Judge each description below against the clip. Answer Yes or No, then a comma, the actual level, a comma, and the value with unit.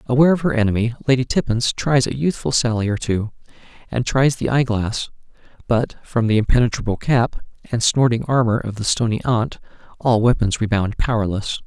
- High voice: No, low, 120 Hz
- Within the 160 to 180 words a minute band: Yes, average, 170 wpm